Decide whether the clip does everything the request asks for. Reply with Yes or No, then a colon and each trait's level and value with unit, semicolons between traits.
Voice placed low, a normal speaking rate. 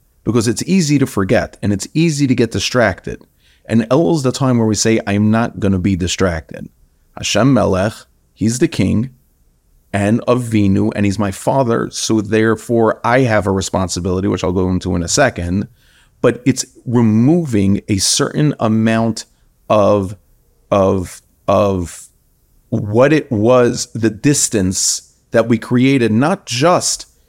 Yes: low, 110 Hz; average, 150 wpm